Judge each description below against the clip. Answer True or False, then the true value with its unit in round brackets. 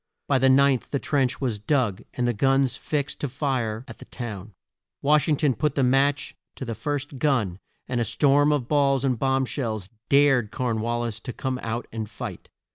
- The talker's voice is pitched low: True (130 Hz)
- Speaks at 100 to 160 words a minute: False (200 wpm)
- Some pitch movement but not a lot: True (3.2 semitones)